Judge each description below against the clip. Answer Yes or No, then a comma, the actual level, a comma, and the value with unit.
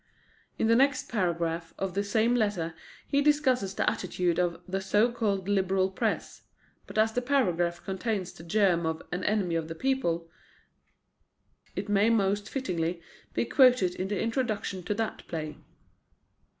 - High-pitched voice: Yes, high, 195 Hz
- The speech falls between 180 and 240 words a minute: No, average, 155 wpm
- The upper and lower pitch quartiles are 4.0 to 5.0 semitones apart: Yes, average, 4.5 semitones